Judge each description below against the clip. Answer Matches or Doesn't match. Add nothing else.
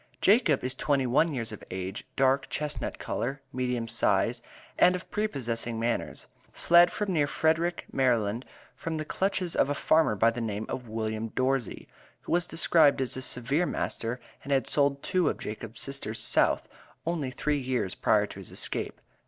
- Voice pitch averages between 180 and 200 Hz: Doesn't match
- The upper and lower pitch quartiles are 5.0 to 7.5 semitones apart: Matches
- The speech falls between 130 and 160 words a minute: Doesn't match